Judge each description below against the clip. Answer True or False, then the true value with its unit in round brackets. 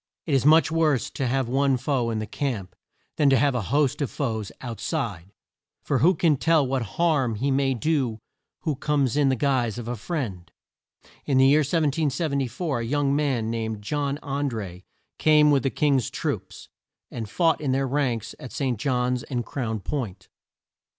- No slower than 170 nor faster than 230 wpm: True (185 wpm)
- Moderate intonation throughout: True (3.8 semitones)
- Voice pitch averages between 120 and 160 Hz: True (135 Hz)